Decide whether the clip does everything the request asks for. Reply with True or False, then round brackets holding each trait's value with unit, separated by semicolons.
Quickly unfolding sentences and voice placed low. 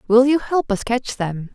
False (235 wpm; 235 Hz)